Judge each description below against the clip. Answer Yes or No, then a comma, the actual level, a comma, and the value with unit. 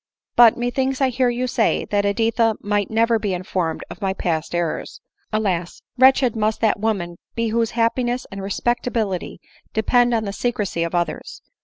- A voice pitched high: Yes, high, 220 Hz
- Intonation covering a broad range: No, average, 3.7 semitones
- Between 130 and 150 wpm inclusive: No, average, 165 wpm